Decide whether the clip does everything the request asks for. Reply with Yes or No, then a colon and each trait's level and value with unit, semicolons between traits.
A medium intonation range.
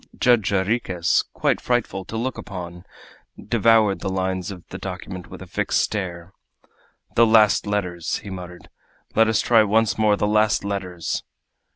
Yes: average, 3.2 semitones